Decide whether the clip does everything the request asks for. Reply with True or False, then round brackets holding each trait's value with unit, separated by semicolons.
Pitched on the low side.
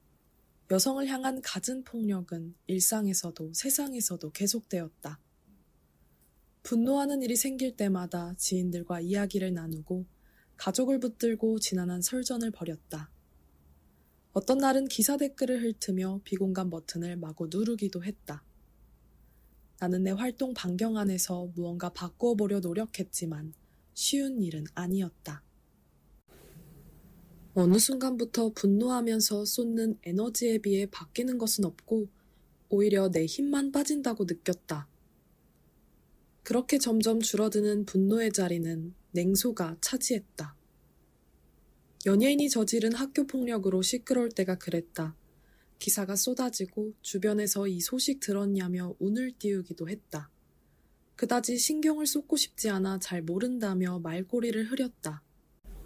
False (195 Hz)